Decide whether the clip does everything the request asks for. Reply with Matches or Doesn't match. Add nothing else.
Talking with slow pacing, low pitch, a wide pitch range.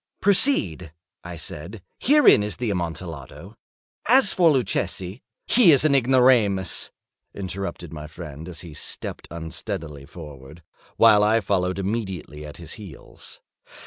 Matches